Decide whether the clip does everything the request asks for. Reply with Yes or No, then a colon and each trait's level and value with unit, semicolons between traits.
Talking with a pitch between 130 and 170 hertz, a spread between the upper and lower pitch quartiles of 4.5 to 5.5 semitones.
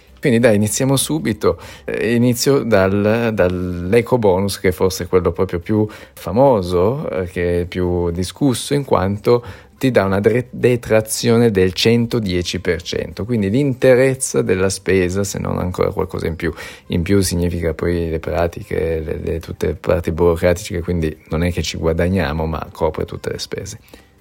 No: very low, 95 Hz; average, 4.8 semitones